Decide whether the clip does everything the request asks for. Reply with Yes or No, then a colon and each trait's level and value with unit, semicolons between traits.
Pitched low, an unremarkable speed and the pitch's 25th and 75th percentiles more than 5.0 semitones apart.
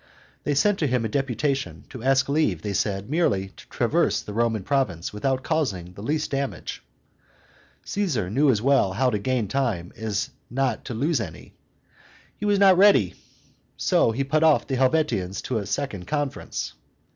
Yes: low, 130 Hz; average, 170 wpm; wide, 5.6 semitones